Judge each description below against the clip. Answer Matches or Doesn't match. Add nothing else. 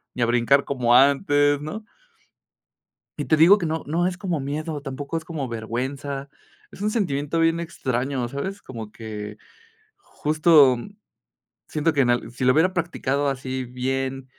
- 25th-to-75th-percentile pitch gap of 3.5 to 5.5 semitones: Matches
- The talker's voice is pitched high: Doesn't match